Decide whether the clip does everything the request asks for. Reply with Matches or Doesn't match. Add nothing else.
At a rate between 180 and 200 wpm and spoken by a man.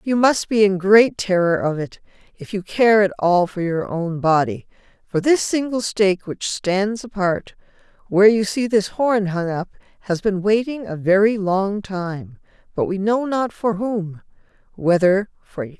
Doesn't match